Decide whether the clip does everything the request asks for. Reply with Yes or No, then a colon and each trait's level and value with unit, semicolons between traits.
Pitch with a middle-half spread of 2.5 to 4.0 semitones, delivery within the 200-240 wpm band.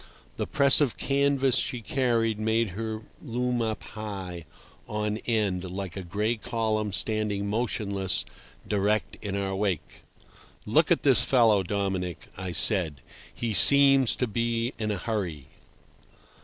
No: average, 3.2 semitones; slow, 135 wpm